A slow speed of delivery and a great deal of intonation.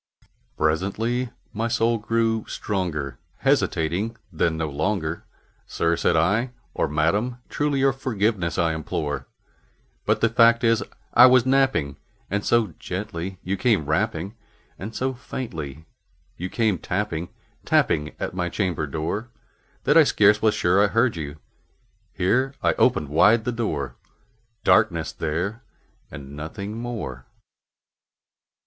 Yes: slow, 130 wpm; wide, 6.3 semitones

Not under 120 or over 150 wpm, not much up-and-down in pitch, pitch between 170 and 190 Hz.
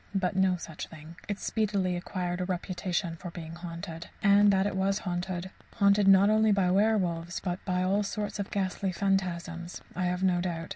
No: average, 185 wpm; narrow, 2.1 semitones; medium, 185 Hz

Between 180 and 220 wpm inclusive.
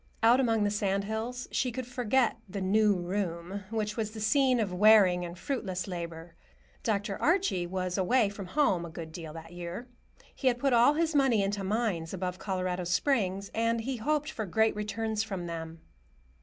Yes: average, 185 wpm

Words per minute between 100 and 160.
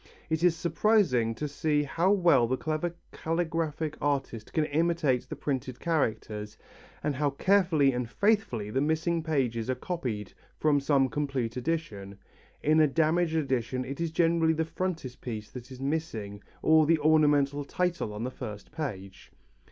Yes: average, 150 wpm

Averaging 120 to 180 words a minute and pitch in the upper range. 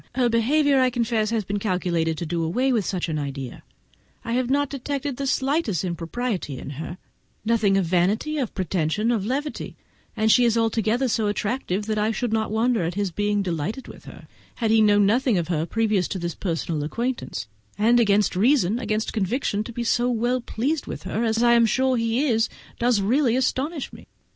No: average, 195 wpm; high, 220 Hz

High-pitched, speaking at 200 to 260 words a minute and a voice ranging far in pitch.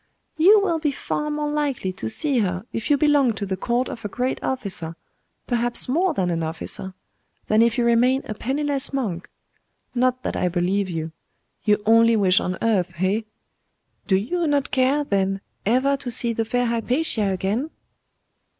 No: high, 235 Hz; average, 175 wpm; wide, 6.0 semitones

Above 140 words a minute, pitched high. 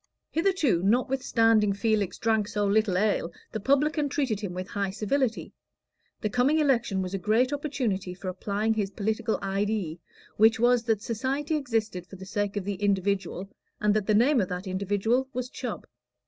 Yes: average, 170 wpm; high, 215 Hz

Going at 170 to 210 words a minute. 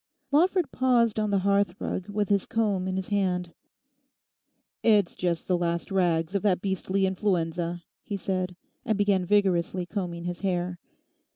No: average, 155 wpm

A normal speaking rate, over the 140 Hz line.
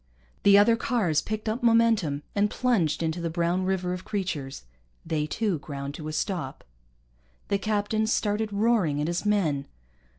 Yes: average, 160 wpm; high, 190 Hz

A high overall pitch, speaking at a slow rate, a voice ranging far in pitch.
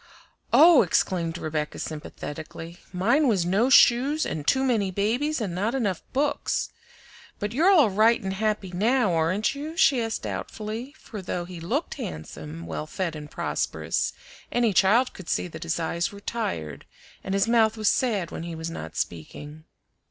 No: high, 200 Hz; average, 165 wpm; wide, 6.3 semitones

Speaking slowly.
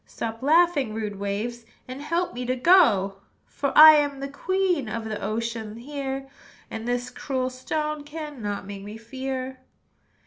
No: average, 150 wpm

